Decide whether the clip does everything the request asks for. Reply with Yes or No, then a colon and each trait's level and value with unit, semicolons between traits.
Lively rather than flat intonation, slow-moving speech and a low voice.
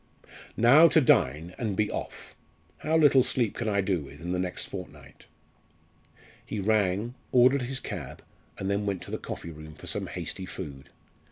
No: wide, 5.7 semitones; average, 175 wpm; low, 100 Hz